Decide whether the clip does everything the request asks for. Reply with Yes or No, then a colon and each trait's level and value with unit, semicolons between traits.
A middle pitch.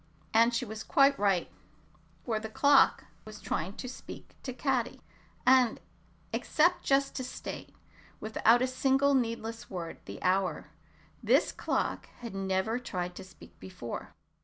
No: high, 230 Hz